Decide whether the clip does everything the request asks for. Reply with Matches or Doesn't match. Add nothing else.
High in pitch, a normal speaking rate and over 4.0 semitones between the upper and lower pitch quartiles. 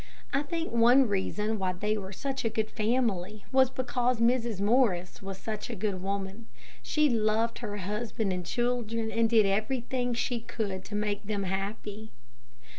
Doesn't match